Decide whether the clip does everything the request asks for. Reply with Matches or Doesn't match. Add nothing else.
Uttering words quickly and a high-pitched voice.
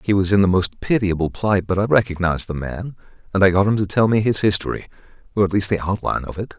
Doesn't match